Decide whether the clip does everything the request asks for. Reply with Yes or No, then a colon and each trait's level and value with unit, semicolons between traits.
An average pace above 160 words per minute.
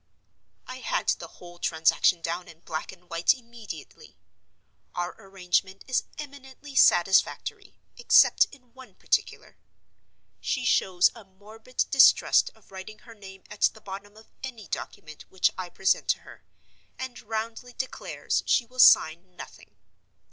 No: average, 140 wpm